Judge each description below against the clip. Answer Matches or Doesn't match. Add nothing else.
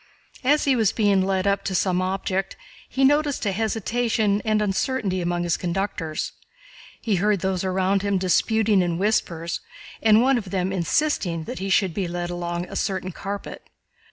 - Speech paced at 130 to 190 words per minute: Matches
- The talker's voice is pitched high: Matches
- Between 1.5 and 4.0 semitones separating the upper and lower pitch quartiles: Matches